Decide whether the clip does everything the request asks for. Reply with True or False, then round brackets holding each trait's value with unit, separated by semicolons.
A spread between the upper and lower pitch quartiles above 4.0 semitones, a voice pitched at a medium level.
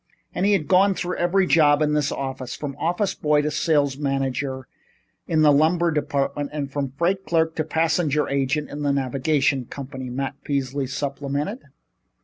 False (2.8 semitones; 145 Hz)